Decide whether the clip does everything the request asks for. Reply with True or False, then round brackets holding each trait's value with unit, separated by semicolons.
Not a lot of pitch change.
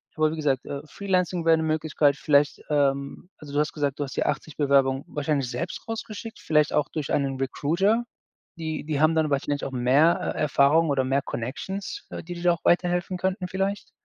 False (3.8 semitones)